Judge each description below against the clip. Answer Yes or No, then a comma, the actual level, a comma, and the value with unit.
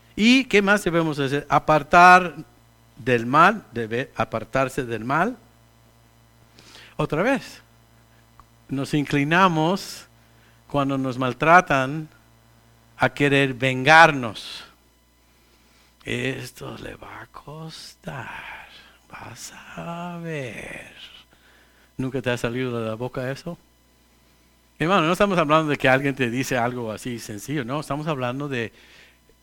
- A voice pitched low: Yes, low, 130 Hz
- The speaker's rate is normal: No, slow, 110 wpm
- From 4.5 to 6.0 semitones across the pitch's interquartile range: Yes, average, 5.1 semitones